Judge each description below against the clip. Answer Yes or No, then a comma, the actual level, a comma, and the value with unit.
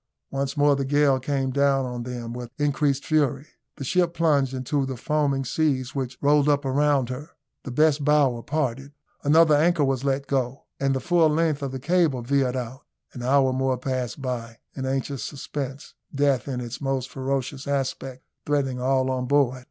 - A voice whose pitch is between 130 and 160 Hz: Yes, low, 135 Hz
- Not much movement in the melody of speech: Yes, narrow, 2.0 semitones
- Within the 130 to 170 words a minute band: No, average, 180 wpm